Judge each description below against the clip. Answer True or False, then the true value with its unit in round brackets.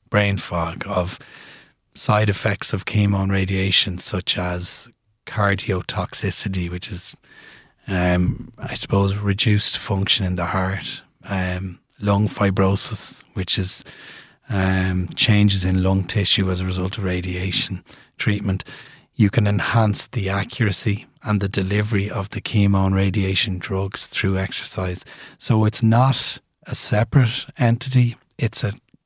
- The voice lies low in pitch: True (100 Hz)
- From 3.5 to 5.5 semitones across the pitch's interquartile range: False (3.0 semitones)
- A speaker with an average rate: False (130 wpm)